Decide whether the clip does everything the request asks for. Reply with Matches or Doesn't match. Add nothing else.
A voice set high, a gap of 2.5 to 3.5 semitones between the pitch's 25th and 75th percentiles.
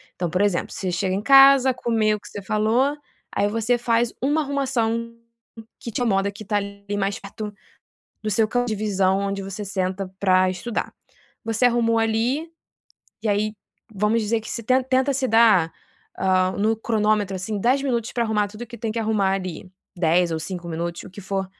Matches